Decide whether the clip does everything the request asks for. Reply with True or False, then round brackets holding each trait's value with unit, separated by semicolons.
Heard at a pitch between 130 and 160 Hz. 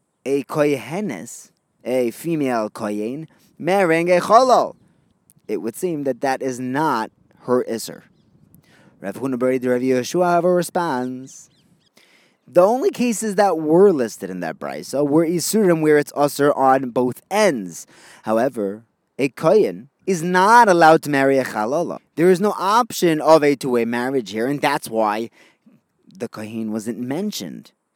True (140 Hz)